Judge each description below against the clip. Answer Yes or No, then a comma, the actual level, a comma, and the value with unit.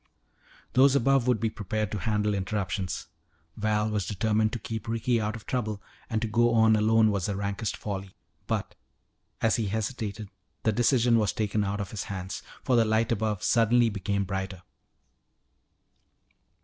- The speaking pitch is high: No, low, 110 Hz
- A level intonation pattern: Yes, narrow, 2.1 semitones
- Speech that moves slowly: No, average, 160 wpm